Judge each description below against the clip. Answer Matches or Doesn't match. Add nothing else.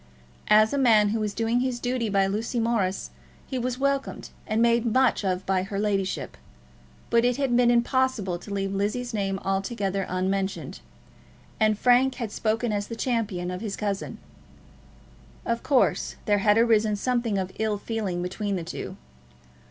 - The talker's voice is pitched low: Doesn't match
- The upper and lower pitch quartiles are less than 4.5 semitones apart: Matches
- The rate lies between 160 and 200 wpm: Matches